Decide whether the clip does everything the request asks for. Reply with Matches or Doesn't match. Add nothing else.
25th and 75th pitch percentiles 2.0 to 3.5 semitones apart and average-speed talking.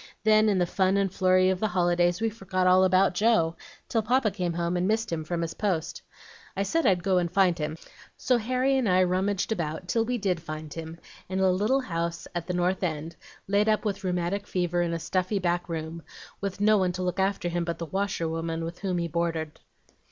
Doesn't match